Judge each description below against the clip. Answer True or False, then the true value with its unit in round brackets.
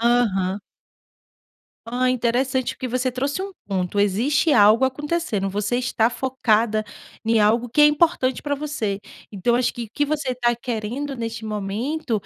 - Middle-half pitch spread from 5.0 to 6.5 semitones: False (3.7 semitones)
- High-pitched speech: True (240 Hz)